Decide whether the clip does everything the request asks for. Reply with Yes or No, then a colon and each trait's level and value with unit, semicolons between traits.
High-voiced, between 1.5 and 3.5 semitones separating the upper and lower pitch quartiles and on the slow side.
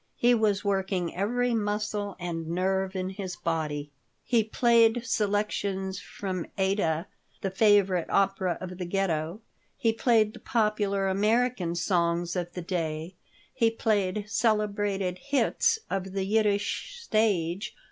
Yes: high, 195 Hz; average, 3.0 semitones; slow, 125 wpm